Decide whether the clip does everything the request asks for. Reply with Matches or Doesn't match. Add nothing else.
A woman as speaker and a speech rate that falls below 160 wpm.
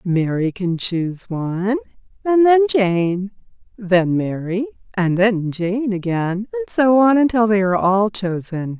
Matches